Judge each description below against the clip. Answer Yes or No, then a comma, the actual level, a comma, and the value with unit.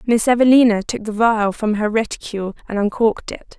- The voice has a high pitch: Yes, high, 220 Hz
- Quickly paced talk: No, average, 185 wpm